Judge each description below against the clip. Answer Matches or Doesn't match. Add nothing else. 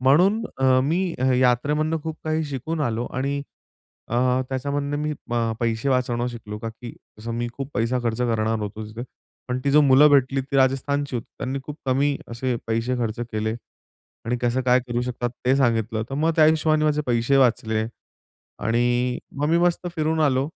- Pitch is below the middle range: Matches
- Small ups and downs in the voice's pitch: Doesn't match